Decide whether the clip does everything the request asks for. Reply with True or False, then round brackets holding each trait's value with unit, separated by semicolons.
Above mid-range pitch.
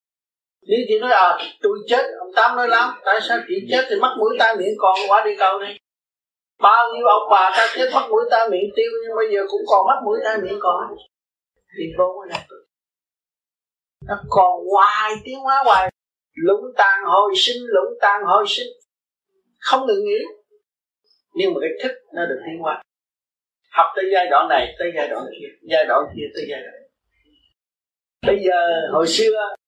True (225 Hz)